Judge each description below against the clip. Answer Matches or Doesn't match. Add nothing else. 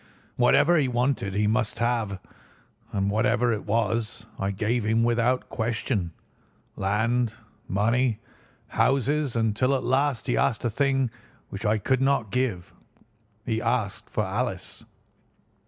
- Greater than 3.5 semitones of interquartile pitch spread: Doesn't match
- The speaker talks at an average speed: Doesn't match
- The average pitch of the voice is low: Matches